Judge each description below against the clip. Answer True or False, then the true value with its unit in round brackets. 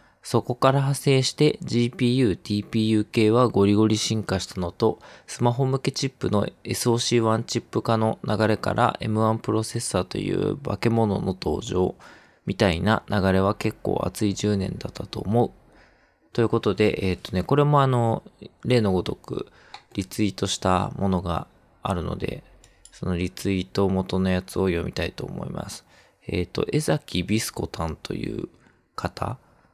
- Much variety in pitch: False (3.8 semitones)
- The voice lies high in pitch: False (110 Hz)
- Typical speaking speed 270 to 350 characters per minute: True (310 characters per minute)